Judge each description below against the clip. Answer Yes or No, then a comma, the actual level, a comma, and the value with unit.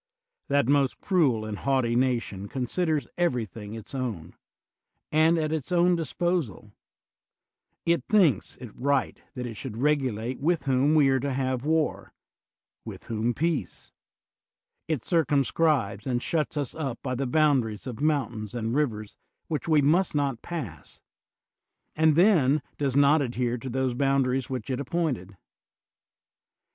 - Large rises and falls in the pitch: No, average, 4.2 semitones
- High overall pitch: No, low, 135 Hz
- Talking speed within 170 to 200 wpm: No, average, 140 wpm